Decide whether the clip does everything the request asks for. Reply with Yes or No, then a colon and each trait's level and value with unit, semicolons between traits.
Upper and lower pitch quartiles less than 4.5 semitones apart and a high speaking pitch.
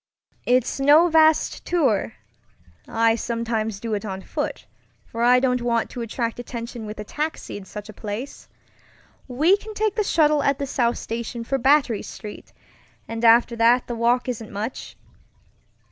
Yes: average, 3.5 semitones; high, 235 Hz